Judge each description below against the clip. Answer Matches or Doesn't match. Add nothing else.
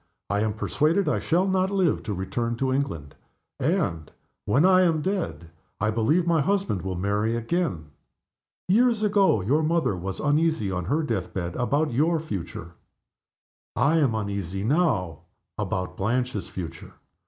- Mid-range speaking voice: Doesn't match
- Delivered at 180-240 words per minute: Doesn't match